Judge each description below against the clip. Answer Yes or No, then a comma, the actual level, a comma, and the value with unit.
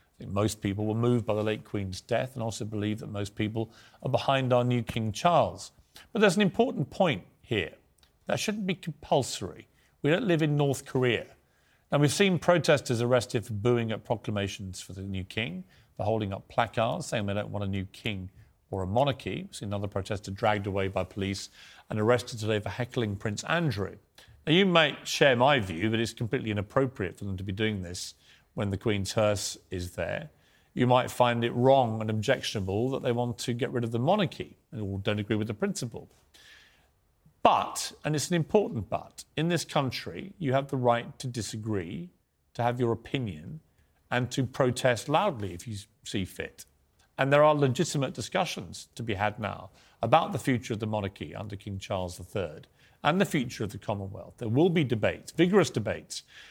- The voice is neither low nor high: No, low, 115 Hz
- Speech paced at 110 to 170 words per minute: No, average, 195 wpm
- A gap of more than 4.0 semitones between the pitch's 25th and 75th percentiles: Yes, average, 4.6 semitones